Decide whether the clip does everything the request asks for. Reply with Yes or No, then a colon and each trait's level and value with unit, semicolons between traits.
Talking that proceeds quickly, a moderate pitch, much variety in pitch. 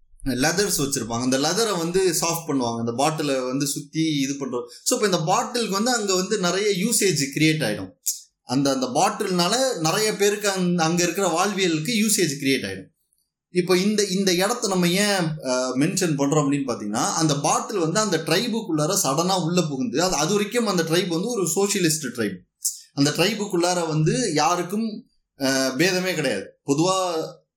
Yes: fast, 150 wpm; medium, 170 Hz; wide, 5.7 semitones